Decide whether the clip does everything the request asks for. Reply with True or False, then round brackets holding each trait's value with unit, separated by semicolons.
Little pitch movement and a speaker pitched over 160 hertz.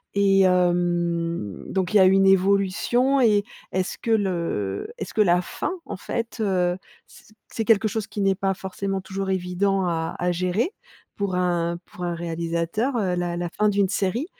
True (2.3 semitones; 190 Hz)